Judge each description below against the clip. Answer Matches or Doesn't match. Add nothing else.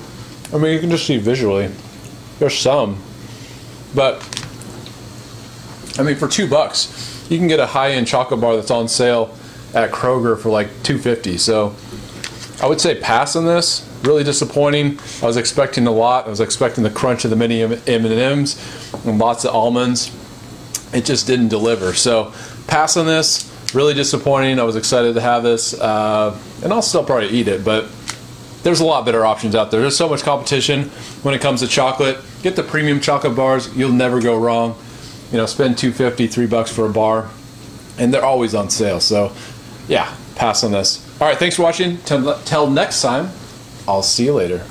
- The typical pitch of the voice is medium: Doesn't match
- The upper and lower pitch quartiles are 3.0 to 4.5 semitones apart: Matches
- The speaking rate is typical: Matches